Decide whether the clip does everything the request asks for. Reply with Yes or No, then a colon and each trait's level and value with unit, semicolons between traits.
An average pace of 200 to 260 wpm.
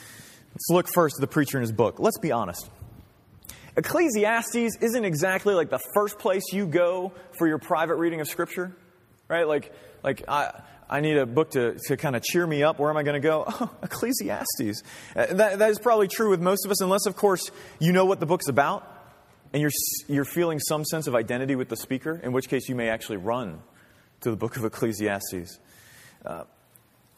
Yes: fast, 205 wpm